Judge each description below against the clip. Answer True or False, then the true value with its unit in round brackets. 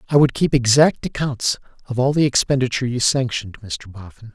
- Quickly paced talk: False (180 wpm)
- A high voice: False (125 Hz)